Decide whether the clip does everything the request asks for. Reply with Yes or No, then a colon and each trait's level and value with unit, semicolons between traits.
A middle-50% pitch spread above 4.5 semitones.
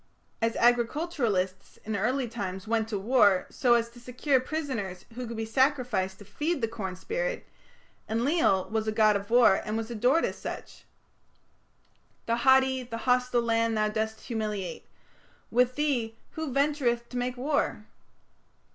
No: average, 3.1 semitones